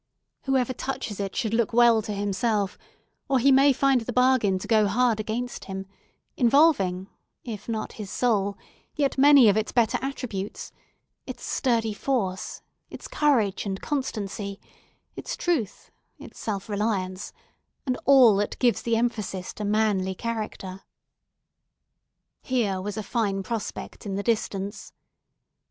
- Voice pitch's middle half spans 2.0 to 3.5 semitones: No, average, 3.9 semitones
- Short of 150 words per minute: Yes, average, 140 wpm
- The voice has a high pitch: Yes, high, 220 Hz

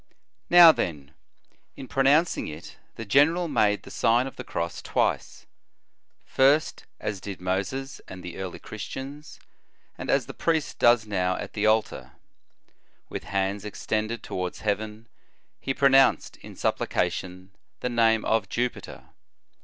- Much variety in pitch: Yes, wide, 5.8 semitones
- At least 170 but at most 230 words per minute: No, slow, 135 wpm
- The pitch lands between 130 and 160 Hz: No, low, 110 Hz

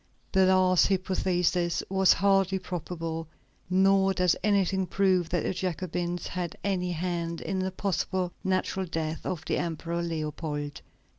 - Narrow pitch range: Yes, narrow, 2.0 semitones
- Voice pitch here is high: No, medium, 180 Hz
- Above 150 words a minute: No, slow, 135 wpm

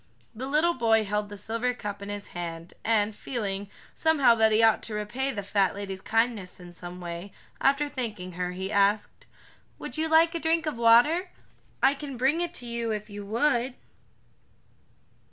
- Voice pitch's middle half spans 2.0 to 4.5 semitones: No, average, 4.9 semitones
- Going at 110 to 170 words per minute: No, average, 180 wpm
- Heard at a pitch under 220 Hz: No, high, 225 Hz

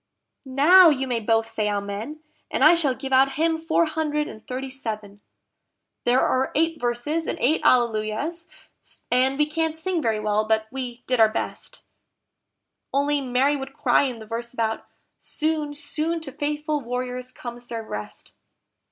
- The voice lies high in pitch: Yes, very high, 260 Hz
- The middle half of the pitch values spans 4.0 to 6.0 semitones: Yes, average, 4.8 semitones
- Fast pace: No, average, 160 wpm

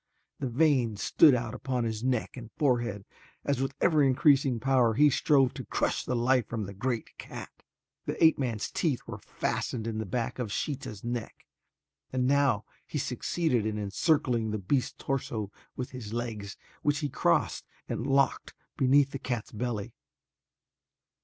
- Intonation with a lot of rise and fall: No, average, 3.4 semitones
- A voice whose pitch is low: Yes, low, 125 Hz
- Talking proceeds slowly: No, average, 160 wpm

